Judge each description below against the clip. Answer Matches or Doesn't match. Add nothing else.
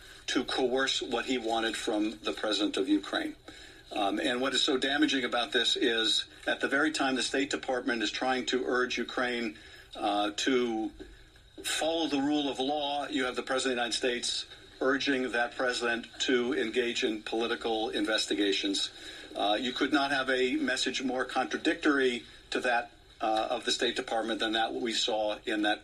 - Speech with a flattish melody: Doesn't match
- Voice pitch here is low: Matches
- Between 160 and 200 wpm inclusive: Matches